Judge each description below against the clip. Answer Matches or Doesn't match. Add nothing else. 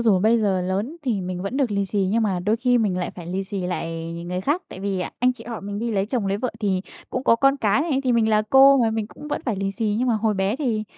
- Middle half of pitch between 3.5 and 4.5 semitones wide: Matches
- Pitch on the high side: Matches